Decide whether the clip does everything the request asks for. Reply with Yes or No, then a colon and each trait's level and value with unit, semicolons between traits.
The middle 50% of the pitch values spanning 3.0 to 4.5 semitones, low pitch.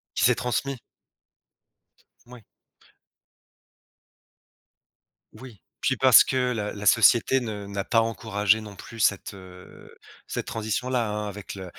Yes: average, 3.3 semitones; low, 110 Hz